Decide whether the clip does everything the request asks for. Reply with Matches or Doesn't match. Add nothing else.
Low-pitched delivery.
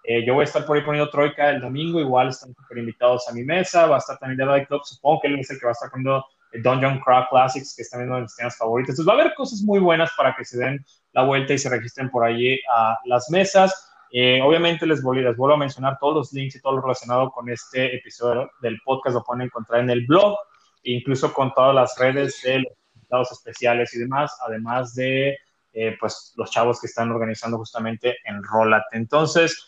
Matches